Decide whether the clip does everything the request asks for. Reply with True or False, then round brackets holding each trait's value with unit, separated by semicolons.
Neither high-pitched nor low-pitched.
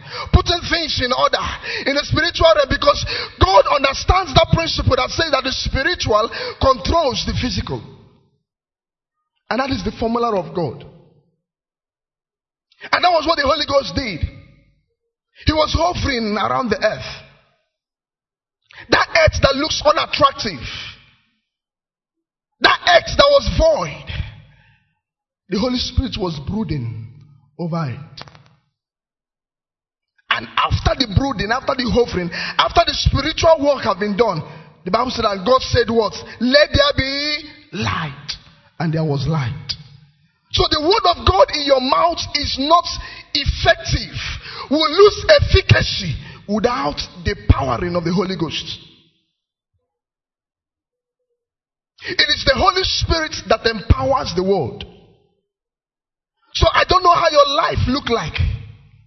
False (255 Hz)